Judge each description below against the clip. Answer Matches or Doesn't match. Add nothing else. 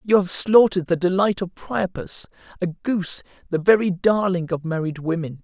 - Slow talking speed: Doesn't match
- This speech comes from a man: Matches